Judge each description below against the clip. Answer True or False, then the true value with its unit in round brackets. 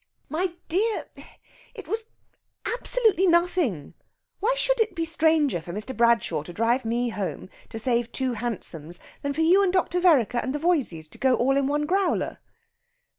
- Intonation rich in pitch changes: True (7.4 semitones)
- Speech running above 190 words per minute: False (170 wpm)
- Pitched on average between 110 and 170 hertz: False (285 Hz)